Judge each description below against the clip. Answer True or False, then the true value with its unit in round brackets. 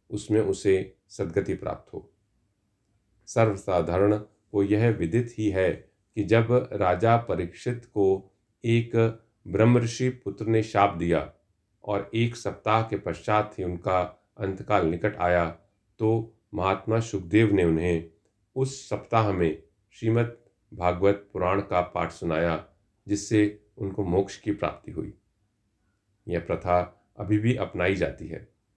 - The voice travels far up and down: False (2.8 semitones)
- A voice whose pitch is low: True (105 Hz)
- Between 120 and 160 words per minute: True (125 wpm)